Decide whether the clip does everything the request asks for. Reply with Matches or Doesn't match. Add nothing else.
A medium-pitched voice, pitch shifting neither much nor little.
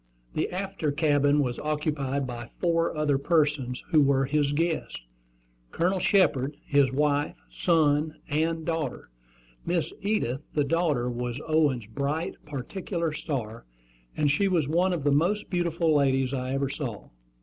Matches